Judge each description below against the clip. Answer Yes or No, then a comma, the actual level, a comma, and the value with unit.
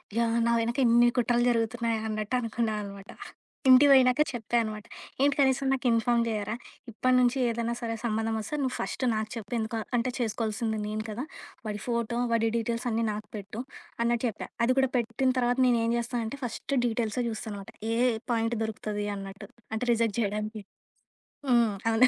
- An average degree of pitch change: No, narrow, 1.9 semitones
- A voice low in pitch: No, high, 230 Hz